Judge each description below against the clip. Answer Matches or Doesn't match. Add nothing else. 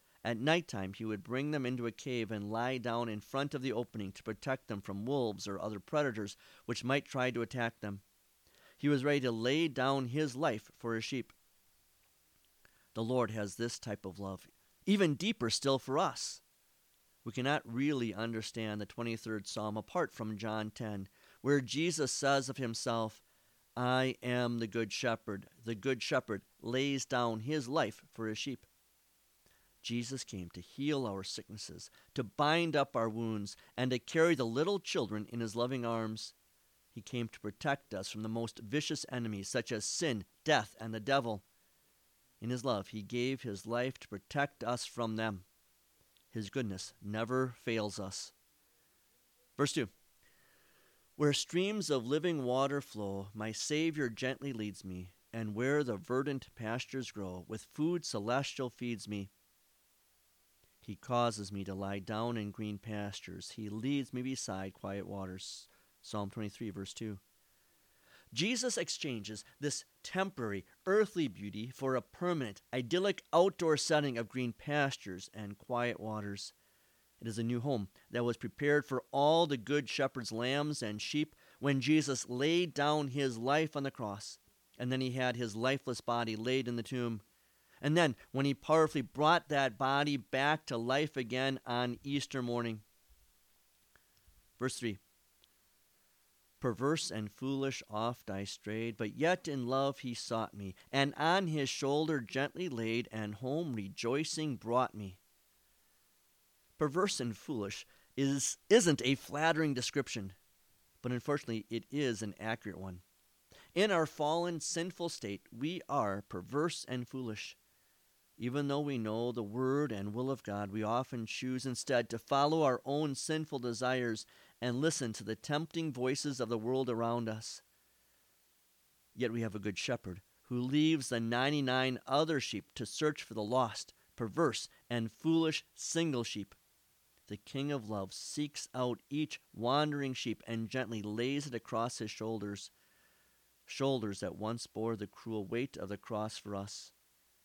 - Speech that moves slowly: Doesn't match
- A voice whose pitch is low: Matches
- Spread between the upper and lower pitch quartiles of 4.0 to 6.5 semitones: Matches